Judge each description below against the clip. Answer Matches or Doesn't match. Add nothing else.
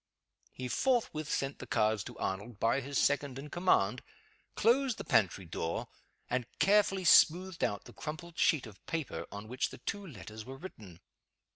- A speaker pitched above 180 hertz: Doesn't match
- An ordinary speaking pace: Matches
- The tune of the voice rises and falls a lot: Matches